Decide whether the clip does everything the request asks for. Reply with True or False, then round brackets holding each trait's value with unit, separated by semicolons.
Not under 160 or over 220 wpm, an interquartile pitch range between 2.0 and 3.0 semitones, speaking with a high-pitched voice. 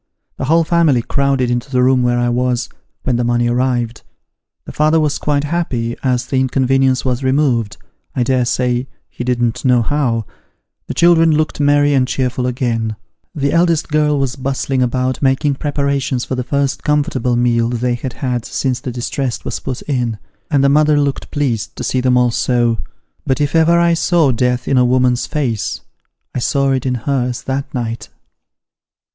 False (180 wpm; 2.7 semitones; 130 Hz)